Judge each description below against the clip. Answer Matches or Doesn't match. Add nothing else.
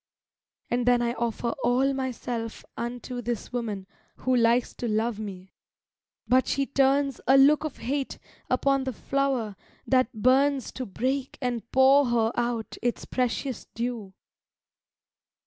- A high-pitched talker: Matches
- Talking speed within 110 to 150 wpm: Matches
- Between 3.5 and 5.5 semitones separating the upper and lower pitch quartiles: Doesn't match